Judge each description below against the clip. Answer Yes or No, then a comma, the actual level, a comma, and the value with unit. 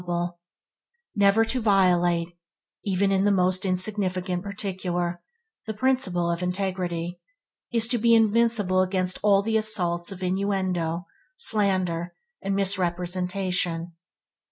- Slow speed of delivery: Yes, slow, 110 wpm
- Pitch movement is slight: Yes, narrow, 2.3 semitones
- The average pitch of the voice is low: No, medium, 185 Hz